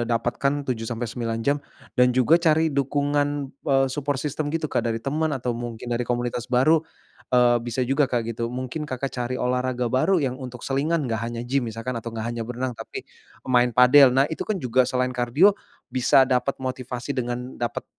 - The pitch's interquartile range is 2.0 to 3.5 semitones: Yes, narrow, 2.5 semitones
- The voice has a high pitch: No, low, 125 Hz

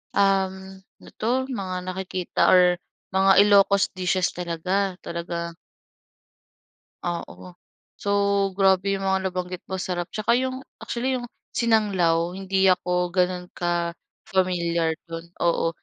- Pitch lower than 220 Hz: Yes, medium, 185 Hz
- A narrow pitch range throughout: Yes, narrow, 1.9 semitones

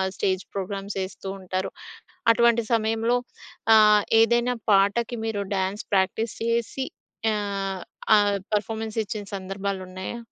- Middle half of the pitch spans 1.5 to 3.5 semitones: Yes, narrow, 2.6 semitones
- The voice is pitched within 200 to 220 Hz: Yes, high, 205 Hz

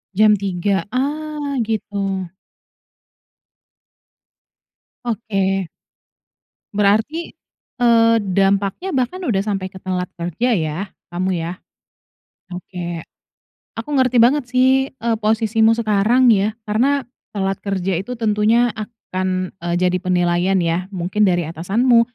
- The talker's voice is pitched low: No, high, 205 Hz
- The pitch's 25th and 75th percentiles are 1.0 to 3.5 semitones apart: No, average, 4.2 semitones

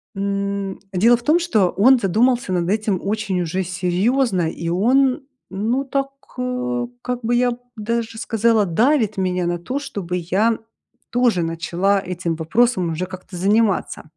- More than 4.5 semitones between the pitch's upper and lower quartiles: Yes, average, 4.9 semitones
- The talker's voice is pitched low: No, high, 205 Hz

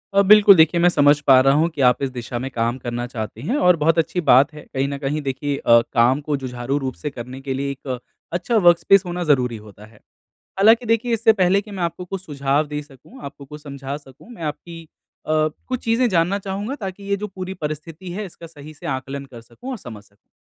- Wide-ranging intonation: Yes, wide, 5.8 semitones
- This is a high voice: No, medium, 150 Hz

